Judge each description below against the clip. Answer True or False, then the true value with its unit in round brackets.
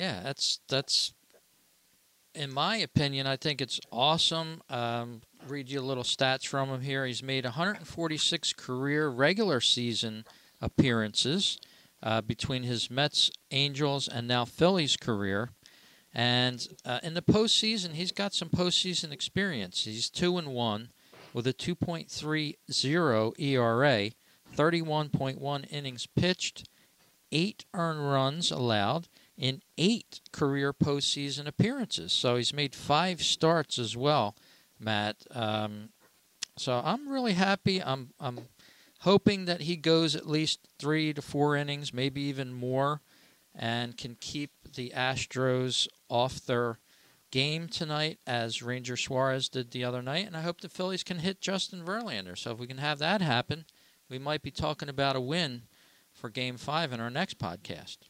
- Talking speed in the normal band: True (145 wpm)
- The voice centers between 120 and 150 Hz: True (140 Hz)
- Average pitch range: True (4.9 semitones)